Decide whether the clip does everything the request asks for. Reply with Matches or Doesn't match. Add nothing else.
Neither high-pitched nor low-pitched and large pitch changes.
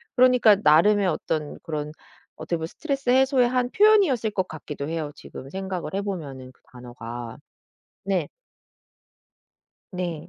Matches